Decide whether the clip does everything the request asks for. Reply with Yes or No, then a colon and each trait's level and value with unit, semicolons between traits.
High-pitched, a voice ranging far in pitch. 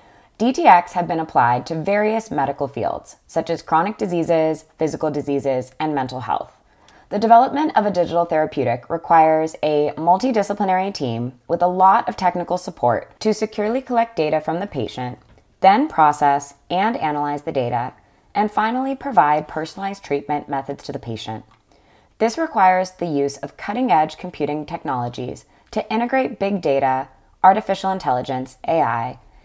No: medium, 160 Hz; wide, 5.8 semitones